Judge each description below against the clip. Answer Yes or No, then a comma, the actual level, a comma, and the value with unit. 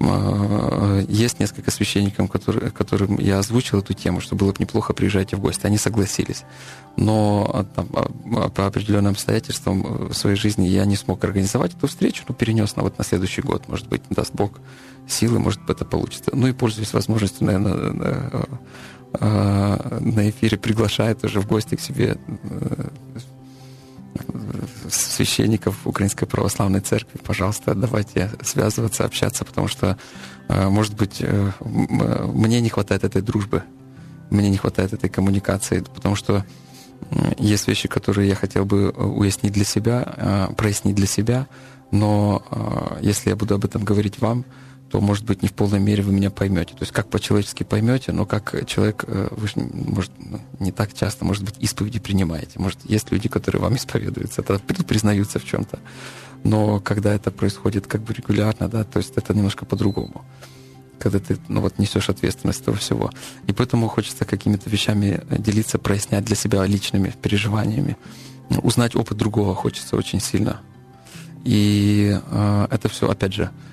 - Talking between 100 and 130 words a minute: No, average, 150 wpm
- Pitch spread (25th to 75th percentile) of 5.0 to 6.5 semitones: No, average, 3.0 semitones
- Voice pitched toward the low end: Yes, low, 105 Hz